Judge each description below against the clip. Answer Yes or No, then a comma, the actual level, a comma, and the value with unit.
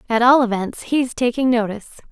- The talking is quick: No, average, 170 wpm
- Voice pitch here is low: No, high, 240 Hz